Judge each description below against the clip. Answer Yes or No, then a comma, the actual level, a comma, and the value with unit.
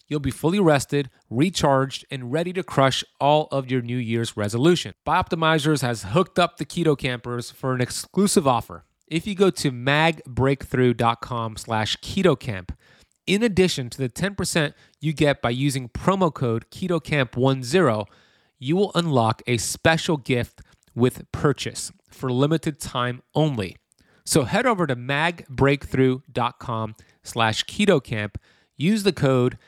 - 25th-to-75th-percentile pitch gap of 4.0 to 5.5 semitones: Yes, average, 5.1 semitones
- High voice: No, low, 135 Hz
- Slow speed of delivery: Yes, slow, 125 wpm